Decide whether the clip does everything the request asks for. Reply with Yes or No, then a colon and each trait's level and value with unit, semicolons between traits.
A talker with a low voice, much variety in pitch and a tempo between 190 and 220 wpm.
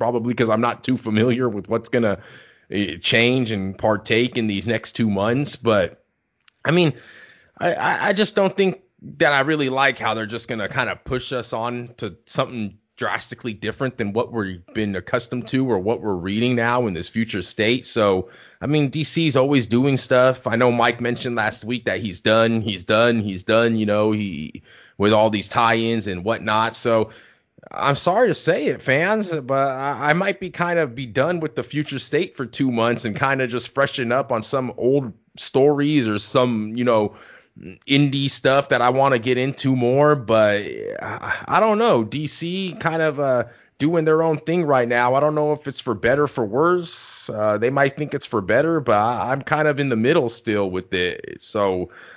No: low, 125 Hz; average, 4.1 semitones; average, 200 wpm